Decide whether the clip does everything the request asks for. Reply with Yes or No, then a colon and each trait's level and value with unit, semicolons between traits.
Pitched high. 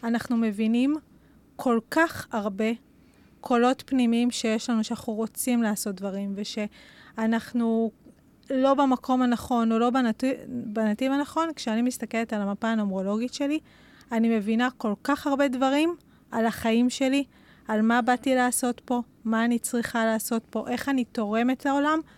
Yes: high, 235 Hz